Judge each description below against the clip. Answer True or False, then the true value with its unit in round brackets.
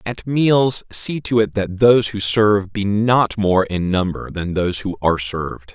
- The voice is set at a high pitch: False (105 Hz)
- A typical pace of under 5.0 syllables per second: True (4.5 syllables/s)